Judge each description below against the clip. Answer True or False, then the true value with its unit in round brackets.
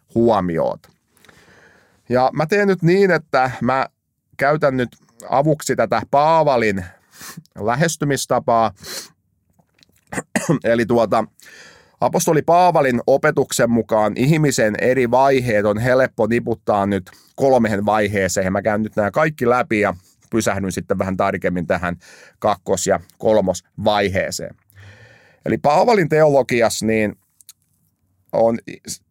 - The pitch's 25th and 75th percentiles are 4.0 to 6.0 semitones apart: True (4.8 semitones)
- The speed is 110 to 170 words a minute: False (100 wpm)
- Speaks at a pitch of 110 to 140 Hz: True (115 Hz)